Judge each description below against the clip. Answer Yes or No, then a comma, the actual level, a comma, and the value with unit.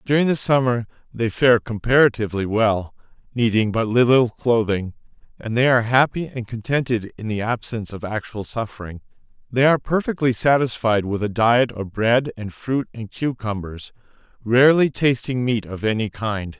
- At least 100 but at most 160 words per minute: Yes, average, 150 wpm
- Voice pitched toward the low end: Yes, low, 115 Hz